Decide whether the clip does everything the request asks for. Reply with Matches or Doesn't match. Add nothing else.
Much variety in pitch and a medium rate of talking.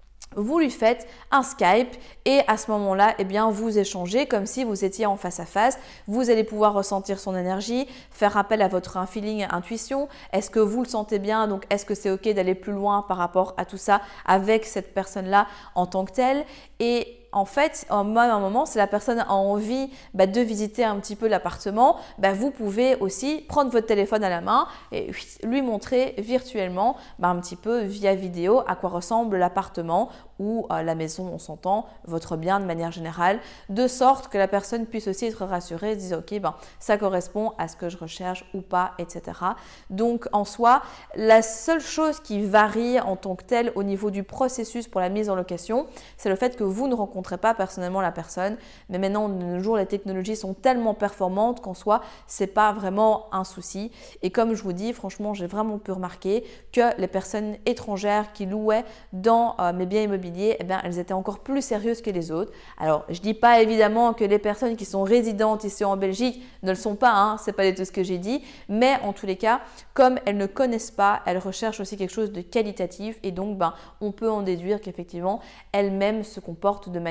Doesn't match